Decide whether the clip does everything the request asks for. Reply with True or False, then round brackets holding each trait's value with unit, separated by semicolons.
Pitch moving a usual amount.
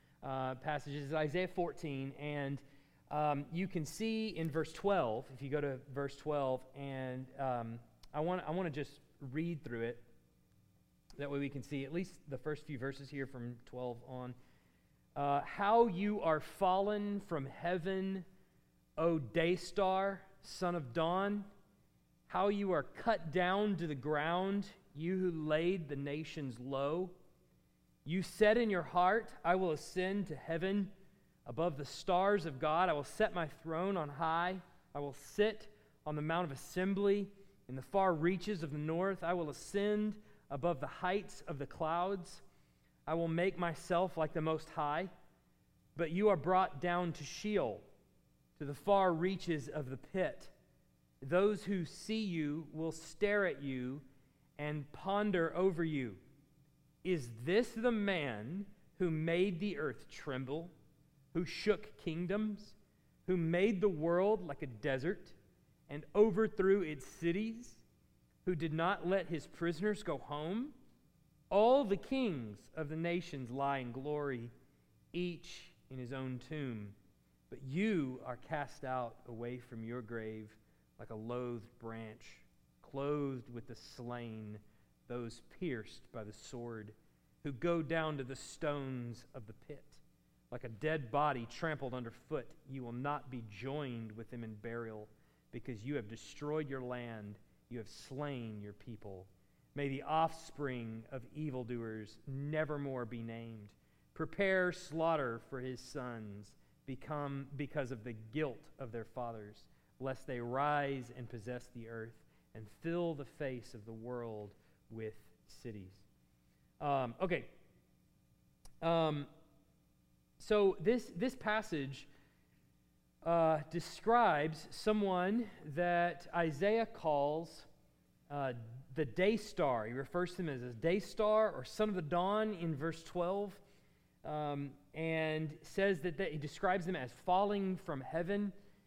False (6.2 semitones)